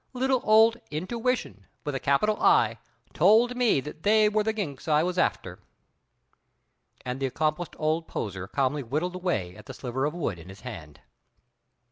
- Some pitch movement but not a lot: No, wide, 8.9 semitones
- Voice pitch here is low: No, medium, 155 Hz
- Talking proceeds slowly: No, average, 165 wpm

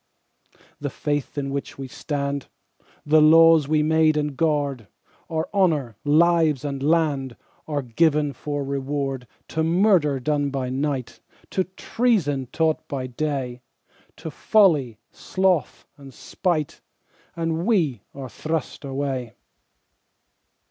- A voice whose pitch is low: No, medium, 145 Hz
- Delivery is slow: Yes, slow, 120 wpm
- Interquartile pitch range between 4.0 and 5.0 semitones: No, average, 2.9 semitones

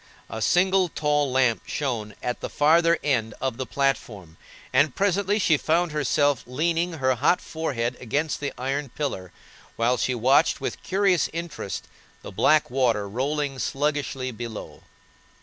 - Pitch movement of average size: Yes, average, 4.4 semitones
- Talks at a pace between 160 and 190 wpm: No, average, 145 wpm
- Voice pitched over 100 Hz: Yes, medium, 140 Hz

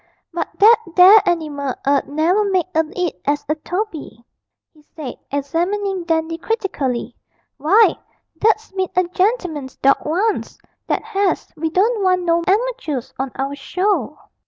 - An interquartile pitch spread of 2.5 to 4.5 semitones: No, average, 5.2 semitones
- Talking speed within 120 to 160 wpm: Yes, average, 140 wpm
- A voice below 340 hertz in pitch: No, very high, 345 Hz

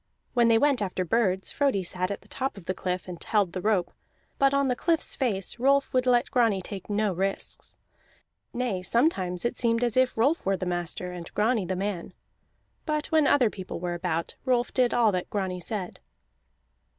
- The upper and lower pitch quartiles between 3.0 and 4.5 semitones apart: No, wide, 5.4 semitones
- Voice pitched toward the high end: Yes, high, 210 Hz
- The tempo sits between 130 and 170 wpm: No, average, 195 wpm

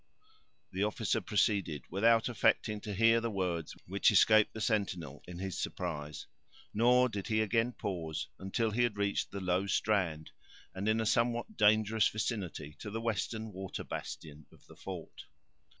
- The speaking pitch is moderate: No, low, 105 Hz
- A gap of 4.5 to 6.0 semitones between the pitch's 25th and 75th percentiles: No, average, 3.4 semitones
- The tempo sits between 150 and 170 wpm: Yes, average, 160 wpm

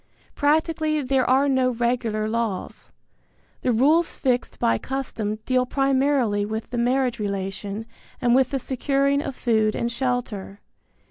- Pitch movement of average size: Yes, average, 3.7 semitones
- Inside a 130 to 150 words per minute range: Yes, slow, 135 wpm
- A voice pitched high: Yes, very high, 250 Hz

